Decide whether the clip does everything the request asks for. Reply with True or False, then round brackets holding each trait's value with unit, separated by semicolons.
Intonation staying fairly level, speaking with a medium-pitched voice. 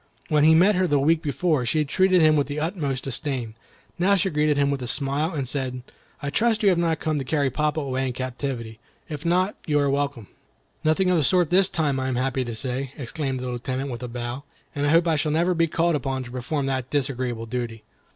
False (3.8 semitones; 145 Hz)